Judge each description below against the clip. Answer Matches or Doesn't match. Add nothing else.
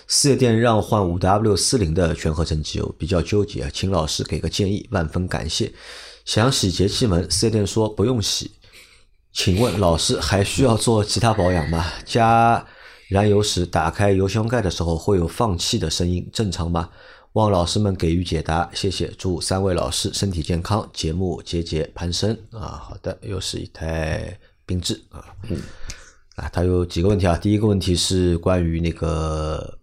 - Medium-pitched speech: Doesn't match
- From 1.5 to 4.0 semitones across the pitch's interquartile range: Matches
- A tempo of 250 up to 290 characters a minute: Matches